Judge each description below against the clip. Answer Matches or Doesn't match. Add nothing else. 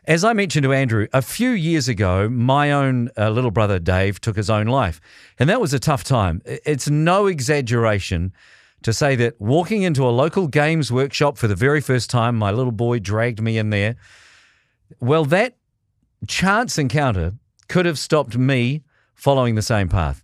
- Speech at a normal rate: Matches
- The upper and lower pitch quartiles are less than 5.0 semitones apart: Doesn't match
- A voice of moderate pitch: Doesn't match